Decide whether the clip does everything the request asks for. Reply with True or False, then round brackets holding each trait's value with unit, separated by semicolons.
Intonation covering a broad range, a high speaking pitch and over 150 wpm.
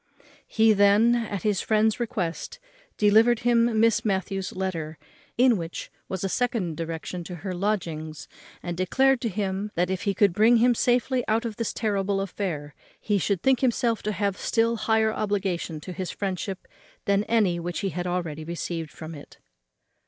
False (4.1 semitones; 200 Hz; 175 wpm)